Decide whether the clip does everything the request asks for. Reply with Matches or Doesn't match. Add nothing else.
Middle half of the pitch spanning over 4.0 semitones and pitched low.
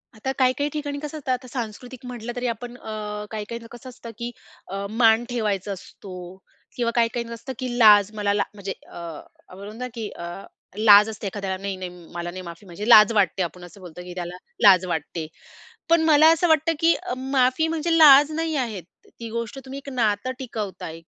Doesn't match